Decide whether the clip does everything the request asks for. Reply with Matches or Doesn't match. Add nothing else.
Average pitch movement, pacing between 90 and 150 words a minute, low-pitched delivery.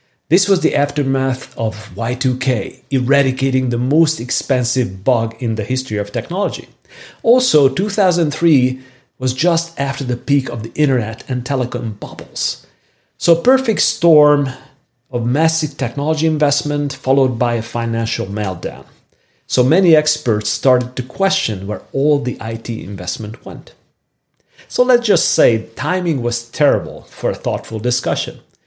Matches